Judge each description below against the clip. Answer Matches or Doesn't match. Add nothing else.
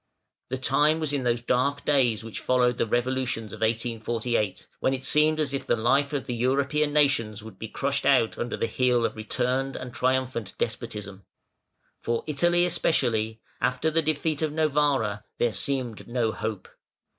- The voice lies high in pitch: Doesn't match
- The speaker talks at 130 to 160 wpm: Doesn't match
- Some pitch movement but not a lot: Matches